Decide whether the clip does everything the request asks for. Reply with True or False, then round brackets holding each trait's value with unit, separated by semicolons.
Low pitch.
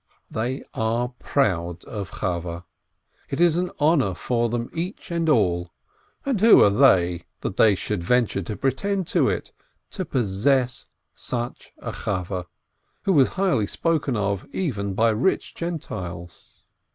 True (115 Hz)